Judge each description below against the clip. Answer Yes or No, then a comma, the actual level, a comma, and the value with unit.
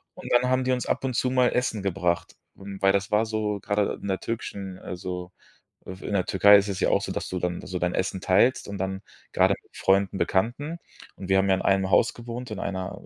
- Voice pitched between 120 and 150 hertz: No, low, 100 Hz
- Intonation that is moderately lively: Yes, average, 3.2 semitones